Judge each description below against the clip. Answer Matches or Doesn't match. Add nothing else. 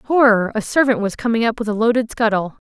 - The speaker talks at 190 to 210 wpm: Doesn't match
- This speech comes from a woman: Matches